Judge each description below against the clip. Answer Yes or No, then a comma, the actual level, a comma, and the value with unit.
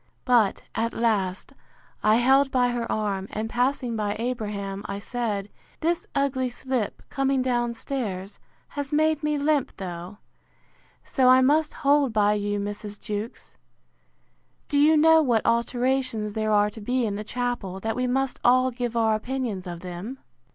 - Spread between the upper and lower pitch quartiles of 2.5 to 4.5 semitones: Yes, average, 4.1 semitones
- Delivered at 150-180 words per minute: Yes, average, 160 wpm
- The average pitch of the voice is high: Yes, high, 240 Hz